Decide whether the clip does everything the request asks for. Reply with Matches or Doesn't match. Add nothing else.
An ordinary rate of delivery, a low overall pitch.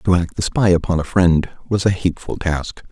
Doesn't match